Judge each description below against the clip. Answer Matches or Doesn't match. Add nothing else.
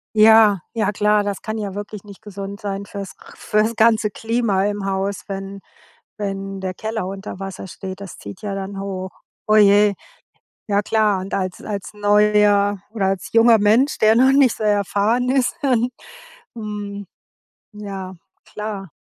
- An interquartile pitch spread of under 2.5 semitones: Matches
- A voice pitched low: Doesn't match